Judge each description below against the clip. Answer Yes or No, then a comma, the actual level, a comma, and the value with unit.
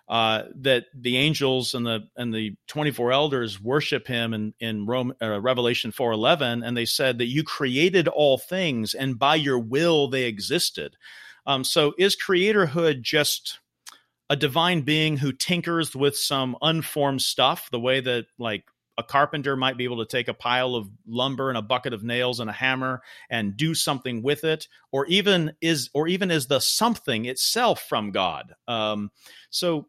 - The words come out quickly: No, average, 180 wpm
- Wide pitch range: No, average, 4.2 semitones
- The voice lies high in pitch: No, low, 130 Hz